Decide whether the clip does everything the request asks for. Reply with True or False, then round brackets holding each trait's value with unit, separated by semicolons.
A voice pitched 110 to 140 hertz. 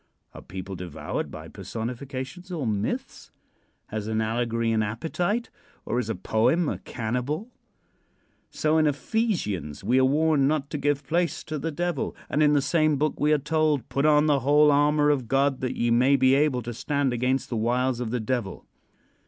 True (135 Hz)